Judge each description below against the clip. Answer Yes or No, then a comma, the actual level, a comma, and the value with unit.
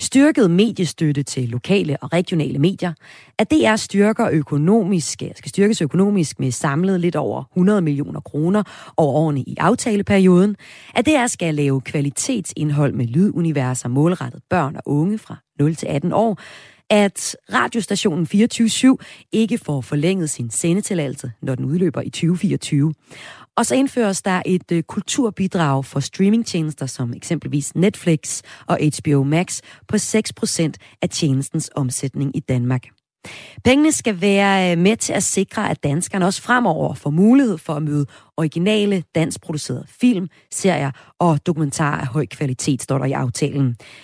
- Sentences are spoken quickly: No, slow, 145 wpm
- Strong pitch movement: Yes, wide, 5.7 semitones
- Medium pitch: Yes, medium, 165 Hz